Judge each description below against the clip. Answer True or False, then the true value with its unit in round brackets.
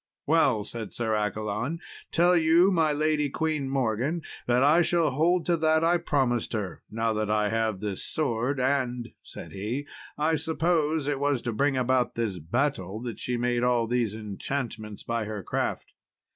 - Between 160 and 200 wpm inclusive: True (170 wpm)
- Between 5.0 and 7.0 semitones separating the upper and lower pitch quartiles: True (5.6 semitones)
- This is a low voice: True (125 Hz)